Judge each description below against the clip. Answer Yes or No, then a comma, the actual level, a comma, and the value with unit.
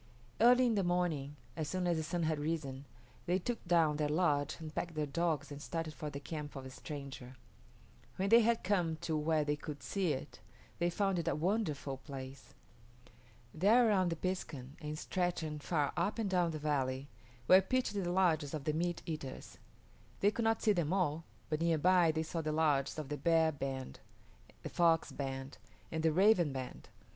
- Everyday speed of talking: Yes, average, 195 wpm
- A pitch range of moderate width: Yes, average, 3.4 semitones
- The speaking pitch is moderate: Yes, medium, 160 Hz